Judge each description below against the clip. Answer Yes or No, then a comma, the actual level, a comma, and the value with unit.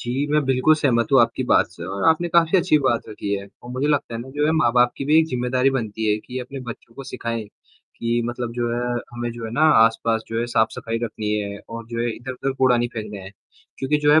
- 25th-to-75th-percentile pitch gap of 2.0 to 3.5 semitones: Yes, average, 2.9 semitones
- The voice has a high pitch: No, low, 120 Hz